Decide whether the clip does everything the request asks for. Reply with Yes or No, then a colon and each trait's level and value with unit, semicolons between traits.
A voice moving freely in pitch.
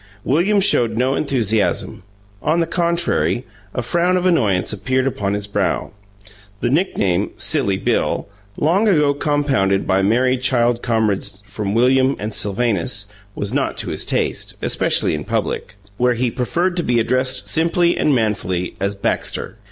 Yes: wide, 6.4 semitones